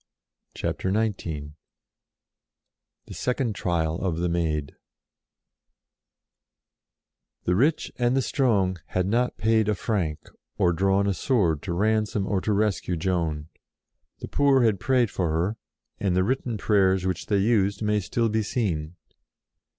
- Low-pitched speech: Yes, low, 100 Hz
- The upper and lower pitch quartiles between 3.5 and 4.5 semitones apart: Yes, average, 4.1 semitones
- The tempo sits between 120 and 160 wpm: Yes, average, 140 wpm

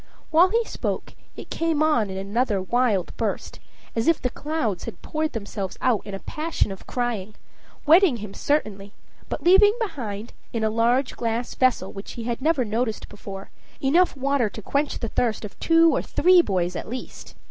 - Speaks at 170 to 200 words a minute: Yes, average, 180 wpm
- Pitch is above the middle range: Yes, high, 240 Hz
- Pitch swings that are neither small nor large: No, wide, 6.7 semitones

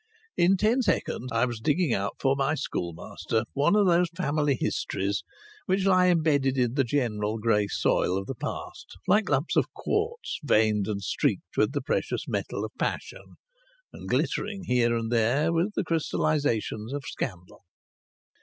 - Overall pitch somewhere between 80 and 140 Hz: Yes, low, 135 Hz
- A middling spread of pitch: No, wide, 7.3 semitones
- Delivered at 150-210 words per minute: Yes, average, 160 wpm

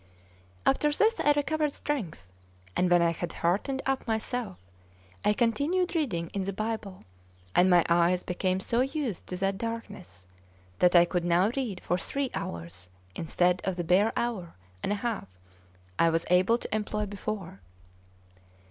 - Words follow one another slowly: No, average, 155 wpm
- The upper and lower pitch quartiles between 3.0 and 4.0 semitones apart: No, wide, 5.4 semitones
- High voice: Yes, high, 195 Hz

